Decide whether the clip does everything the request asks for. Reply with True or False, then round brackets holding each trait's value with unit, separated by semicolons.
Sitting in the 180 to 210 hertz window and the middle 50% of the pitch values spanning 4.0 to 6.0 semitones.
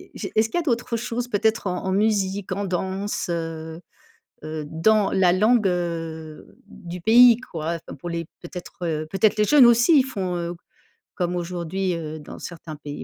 True (185 Hz; 4.5 semitones)